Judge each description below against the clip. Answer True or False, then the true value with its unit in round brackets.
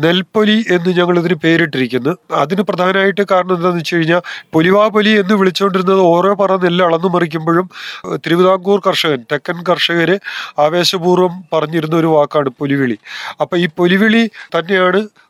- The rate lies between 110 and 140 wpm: True (125 wpm)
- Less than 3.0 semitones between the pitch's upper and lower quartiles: True (2.5 semitones)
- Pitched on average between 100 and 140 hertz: False (180 Hz)